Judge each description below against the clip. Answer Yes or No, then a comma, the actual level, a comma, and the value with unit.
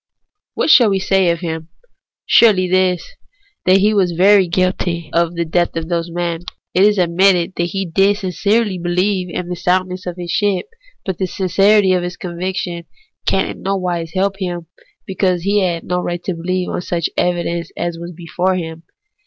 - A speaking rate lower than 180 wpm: No, average, 185 wpm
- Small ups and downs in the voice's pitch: Yes, narrow, 1.9 semitones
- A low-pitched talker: No, medium, 180 Hz